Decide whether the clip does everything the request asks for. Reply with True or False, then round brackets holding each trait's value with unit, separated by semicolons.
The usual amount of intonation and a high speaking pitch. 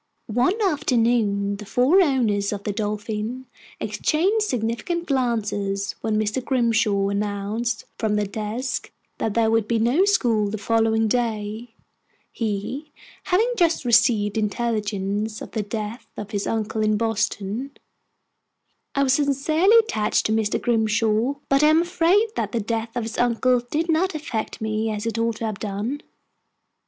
True (3.6 semitones; 225 Hz)